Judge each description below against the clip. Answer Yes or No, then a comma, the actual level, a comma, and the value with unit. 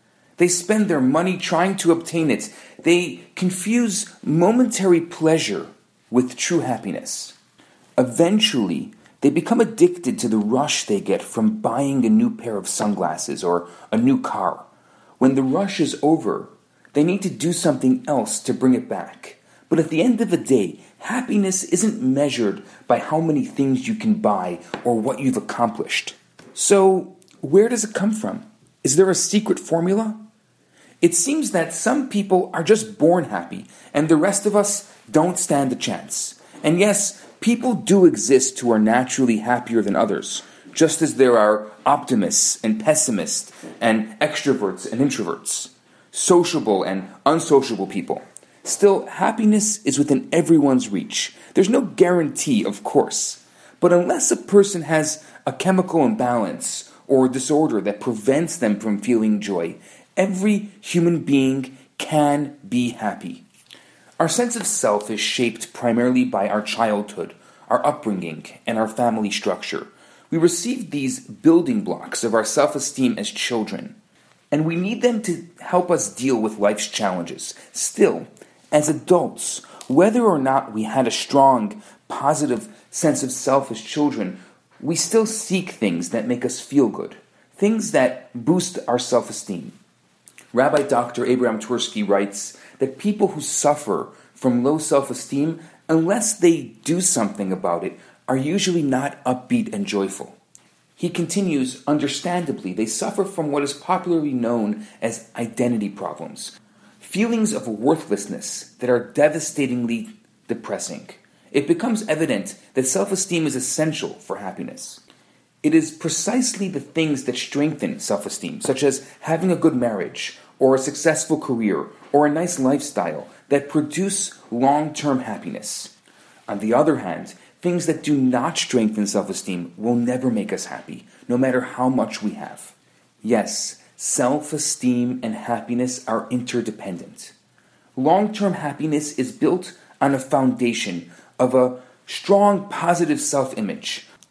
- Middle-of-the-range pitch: Yes, medium, 155 Hz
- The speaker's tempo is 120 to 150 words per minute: Yes, average, 145 wpm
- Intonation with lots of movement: Yes, wide, 7.3 semitones